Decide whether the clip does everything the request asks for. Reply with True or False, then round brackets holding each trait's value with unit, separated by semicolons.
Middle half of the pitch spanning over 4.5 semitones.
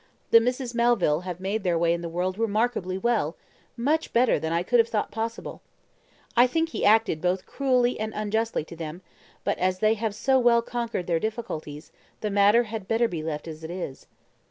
True (5.1 semitones)